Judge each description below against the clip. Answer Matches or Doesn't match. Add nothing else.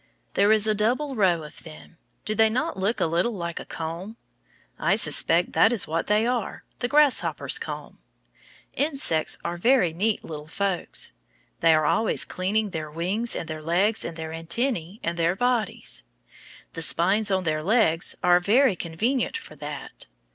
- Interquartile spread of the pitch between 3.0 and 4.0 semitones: Doesn't match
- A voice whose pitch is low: Doesn't match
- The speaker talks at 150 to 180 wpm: Matches